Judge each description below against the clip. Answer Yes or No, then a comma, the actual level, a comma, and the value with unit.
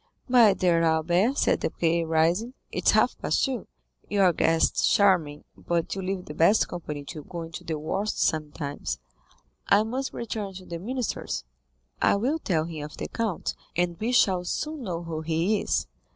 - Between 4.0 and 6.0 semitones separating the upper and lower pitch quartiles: Yes, average, 4.7 semitones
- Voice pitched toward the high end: No, medium, 175 Hz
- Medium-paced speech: Yes, average, 180 wpm